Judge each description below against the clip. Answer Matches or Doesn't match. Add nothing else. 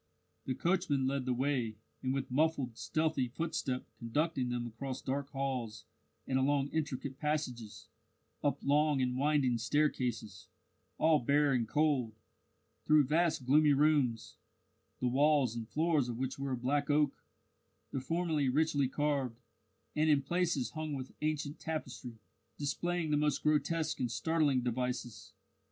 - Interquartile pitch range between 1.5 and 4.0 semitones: Matches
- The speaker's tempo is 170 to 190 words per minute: Doesn't match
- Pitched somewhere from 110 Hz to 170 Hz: Matches